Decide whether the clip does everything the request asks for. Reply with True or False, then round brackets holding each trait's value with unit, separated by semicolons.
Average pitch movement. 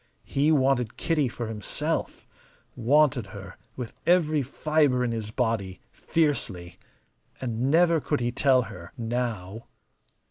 True (4.9 semitones)